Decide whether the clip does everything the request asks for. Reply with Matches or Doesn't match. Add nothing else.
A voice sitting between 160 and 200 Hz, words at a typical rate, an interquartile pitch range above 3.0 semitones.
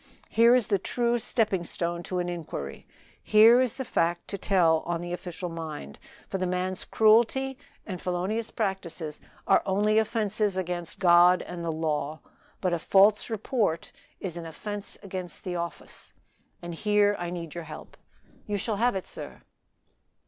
Matches